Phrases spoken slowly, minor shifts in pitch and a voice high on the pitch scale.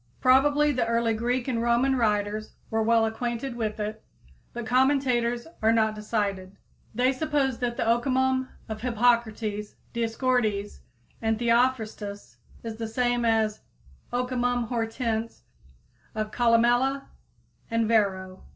Yes: slow, 120 wpm; narrow, 2.2 semitones; high, 230 Hz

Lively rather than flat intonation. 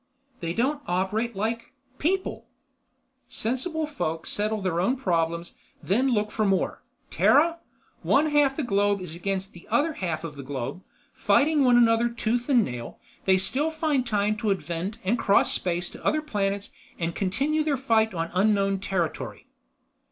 Yes: wide, 6.3 semitones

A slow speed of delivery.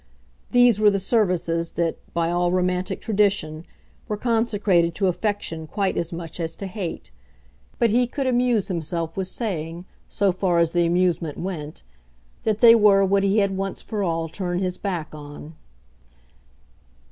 No: average, 160 wpm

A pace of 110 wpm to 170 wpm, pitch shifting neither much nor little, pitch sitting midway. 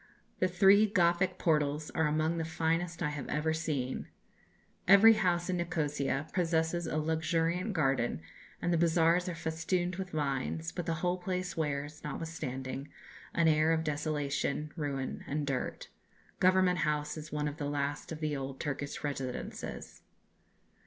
Yes: average, 150 wpm; average, 3.0 semitones; medium, 160 Hz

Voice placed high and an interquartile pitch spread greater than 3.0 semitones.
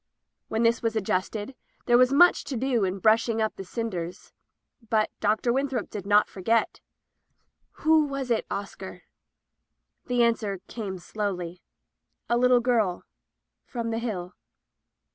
Yes: high, 225 Hz; average, 3.6 semitones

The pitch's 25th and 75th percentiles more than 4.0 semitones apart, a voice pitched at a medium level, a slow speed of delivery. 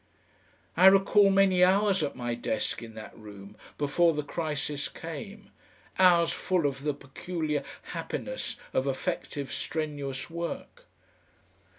Yes: average, 5.1 semitones; medium, 155 Hz; slow, 120 wpm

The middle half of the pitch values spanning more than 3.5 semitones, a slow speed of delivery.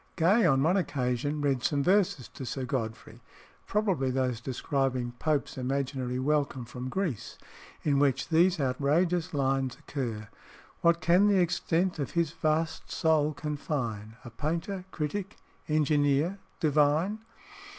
Yes: average, 4.4 semitones; slow, 130 wpm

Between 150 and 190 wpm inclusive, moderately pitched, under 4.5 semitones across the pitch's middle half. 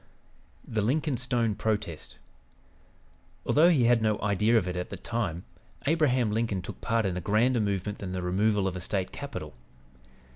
No: average, 170 wpm; low, 105 Hz; average, 3.9 semitones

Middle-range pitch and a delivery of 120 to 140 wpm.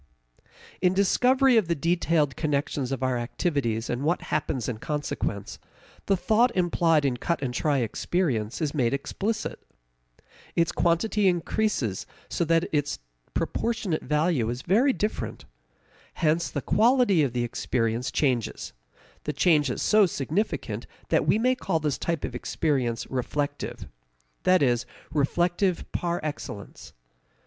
Yes: medium, 155 Hz; slow, 135 wpm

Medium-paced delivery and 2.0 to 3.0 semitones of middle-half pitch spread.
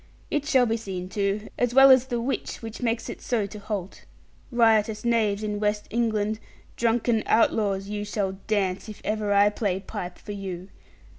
Yes: average, 175 wpm; narrow, 2.4 semitones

